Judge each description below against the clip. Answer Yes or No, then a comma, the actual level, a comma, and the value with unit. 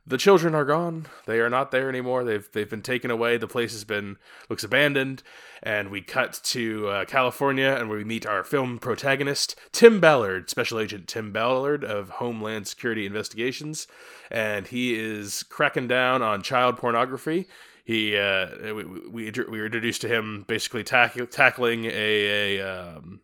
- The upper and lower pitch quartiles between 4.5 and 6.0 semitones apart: No, average, 3.5 semitones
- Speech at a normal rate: Yes, average, 170 wpm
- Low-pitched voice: Yes, low, 115 Hz